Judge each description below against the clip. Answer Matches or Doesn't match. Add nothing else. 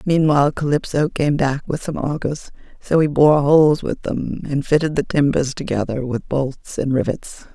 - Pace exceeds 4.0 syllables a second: Matches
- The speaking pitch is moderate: Matches